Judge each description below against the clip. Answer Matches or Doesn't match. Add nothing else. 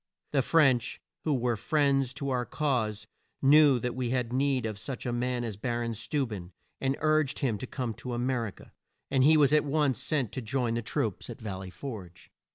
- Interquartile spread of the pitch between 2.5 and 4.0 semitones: Matches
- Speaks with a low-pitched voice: Matches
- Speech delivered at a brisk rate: Matches